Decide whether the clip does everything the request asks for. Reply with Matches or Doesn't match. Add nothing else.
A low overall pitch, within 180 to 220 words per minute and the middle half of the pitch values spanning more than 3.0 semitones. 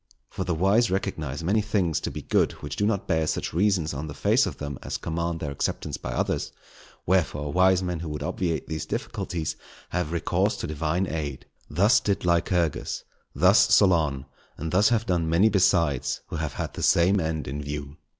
Matches